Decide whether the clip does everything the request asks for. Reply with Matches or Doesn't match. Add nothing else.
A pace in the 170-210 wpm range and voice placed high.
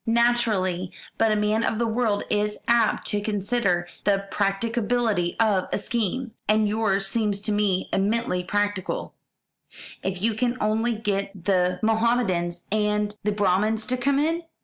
Doesn't match